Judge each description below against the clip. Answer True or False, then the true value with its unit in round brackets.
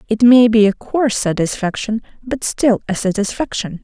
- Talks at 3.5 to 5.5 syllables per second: True (5.0 syllables/s)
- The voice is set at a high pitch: True (220 Hz)